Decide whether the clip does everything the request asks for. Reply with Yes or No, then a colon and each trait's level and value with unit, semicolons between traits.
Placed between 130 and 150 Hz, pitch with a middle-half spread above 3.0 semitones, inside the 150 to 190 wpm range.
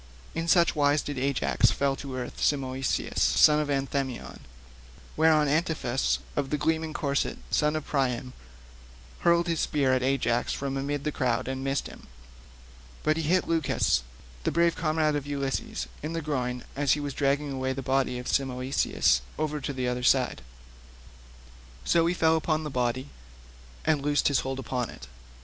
No: medium, 140 Hz; average, 2.7 semitones; average, 165 wpm